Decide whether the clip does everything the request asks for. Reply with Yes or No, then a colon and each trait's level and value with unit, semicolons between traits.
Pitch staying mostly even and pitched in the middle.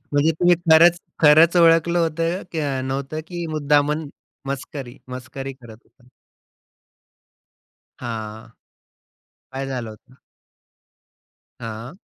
No: average, 4.2 semitones; medium, 145 Hz